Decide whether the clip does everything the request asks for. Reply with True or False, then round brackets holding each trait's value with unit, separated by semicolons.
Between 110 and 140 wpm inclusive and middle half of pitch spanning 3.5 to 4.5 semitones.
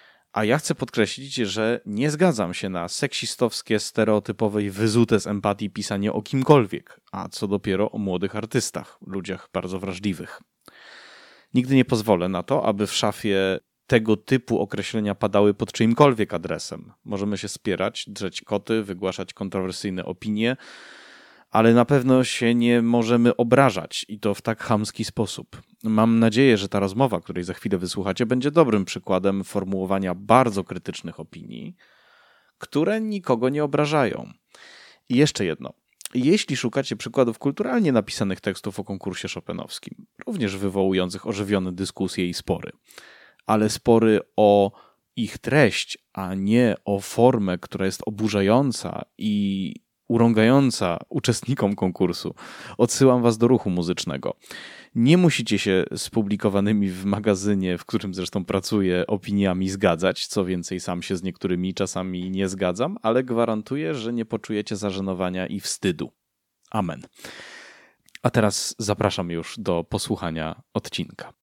True (135 wpm; 3.8 semitones)